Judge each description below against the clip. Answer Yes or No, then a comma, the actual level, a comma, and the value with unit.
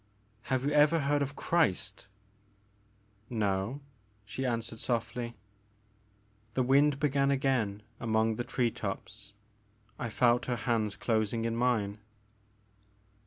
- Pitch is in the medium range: No, low, 115 Hz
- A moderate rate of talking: No, slow, 120 wpm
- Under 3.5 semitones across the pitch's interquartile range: No, average, 3.9 semitones